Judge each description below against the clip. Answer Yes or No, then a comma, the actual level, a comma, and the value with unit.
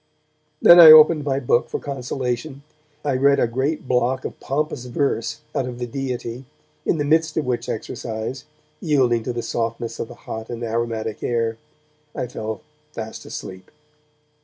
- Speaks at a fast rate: No, average, 165 wpm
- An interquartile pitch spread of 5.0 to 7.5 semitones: No, average, 3.2 semitones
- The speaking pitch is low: Yes, low, 125 Hz